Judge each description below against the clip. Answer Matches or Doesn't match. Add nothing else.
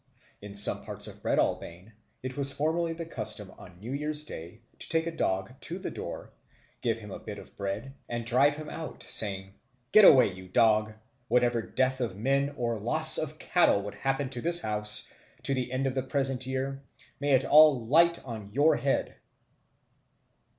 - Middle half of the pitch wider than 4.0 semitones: Matches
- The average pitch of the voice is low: Matches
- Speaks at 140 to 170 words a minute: Doesn't match